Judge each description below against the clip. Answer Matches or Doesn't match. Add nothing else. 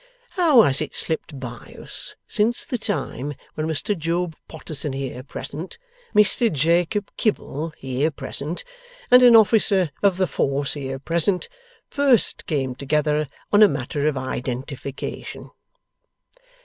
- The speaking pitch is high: Doesn't match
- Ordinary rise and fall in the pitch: Doesn't match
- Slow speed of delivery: Matches